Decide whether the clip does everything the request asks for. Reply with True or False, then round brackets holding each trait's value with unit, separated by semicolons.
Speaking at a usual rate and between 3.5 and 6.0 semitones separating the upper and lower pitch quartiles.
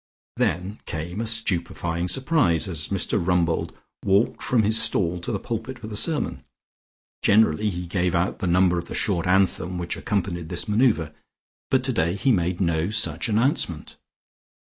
True (160 wpm; 4.2 semitones)